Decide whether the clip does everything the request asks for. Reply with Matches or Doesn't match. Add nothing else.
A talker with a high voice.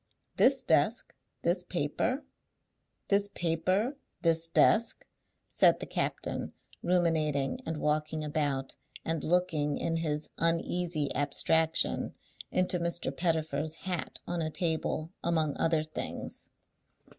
Doesn't match